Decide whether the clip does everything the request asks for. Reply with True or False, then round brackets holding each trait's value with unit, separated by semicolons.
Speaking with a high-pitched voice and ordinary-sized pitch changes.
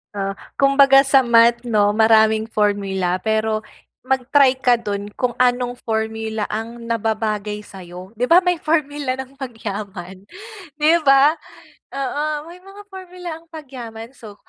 True (235 Hz; 4.3 semitones)